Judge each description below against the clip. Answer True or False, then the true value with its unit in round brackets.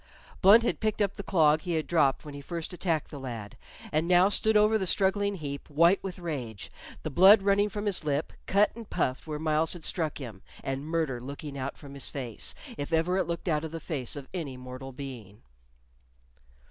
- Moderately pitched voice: True (160 Hz)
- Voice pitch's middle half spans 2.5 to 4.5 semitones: False (5.3 semitones)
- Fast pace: True (210 wpm)